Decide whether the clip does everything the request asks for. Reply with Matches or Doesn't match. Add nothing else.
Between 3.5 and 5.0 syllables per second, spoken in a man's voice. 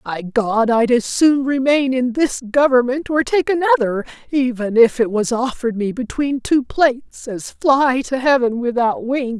Doesn't match